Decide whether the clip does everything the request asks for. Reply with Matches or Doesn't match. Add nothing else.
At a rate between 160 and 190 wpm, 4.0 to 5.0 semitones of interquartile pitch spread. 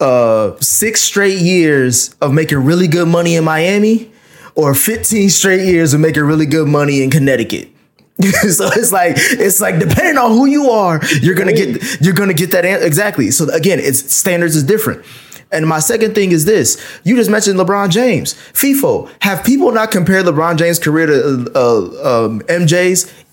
Matches